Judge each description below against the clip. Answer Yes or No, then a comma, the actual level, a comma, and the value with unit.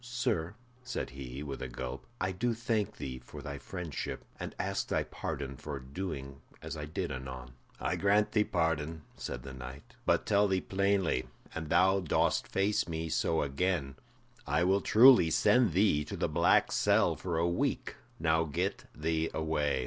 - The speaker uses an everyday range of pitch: No, wide, 5.8 semitones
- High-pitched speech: No, very low, 80 Hz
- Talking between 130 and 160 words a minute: No, average, 170 wpm